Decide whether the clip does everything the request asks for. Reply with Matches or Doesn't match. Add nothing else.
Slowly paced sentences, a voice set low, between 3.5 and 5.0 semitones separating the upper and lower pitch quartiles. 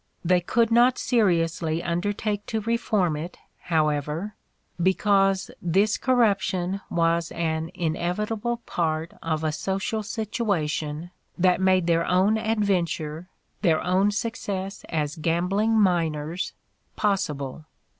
Doesn't match